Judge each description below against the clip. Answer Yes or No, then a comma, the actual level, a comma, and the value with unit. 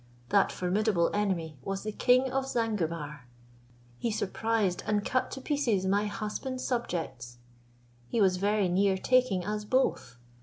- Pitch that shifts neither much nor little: Yes, average, 4.2 semitones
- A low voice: No, high, 205 Hz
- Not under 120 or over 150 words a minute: Yes, average, 140 wpm